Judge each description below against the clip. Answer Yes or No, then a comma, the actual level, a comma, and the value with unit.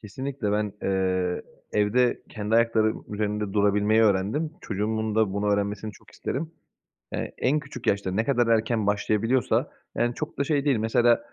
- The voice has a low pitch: Yes, low, 110 Hz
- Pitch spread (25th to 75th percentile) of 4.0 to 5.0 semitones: No, average, 2.7 semitones